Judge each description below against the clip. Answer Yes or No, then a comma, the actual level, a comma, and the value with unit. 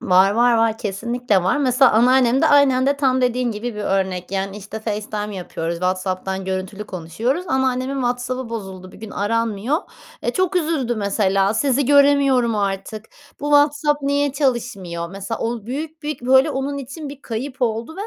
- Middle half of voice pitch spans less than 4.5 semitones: No, average, 5.3 semitones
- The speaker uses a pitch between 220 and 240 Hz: Yes, high, 235 Hz